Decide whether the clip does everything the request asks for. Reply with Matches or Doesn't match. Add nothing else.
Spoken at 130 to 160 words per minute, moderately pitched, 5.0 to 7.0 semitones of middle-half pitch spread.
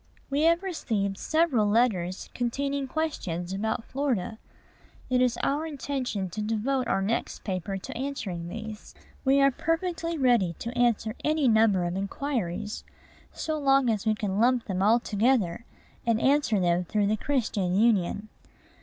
Doesn't match